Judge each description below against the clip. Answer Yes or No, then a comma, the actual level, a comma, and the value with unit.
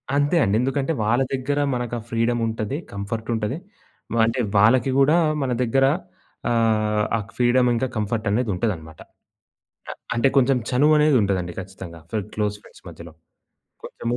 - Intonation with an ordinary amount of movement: Yes, average, 3.7 semitones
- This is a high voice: No, low, 115 Hz